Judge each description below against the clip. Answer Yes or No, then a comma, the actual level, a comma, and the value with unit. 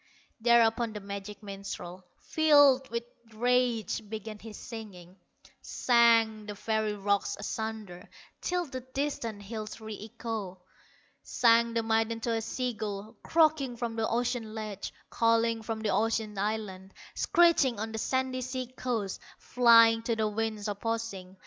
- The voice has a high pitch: Yes, high, 225 Hz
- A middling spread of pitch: No, narrow, 2.2 semitones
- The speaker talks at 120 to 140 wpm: Yes, slow, 135 wpm